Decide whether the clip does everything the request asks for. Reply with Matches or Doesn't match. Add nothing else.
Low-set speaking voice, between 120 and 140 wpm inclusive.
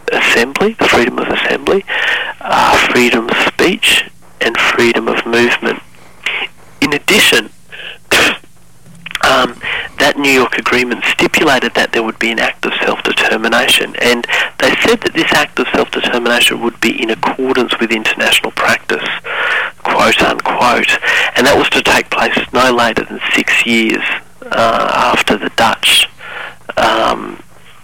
Matches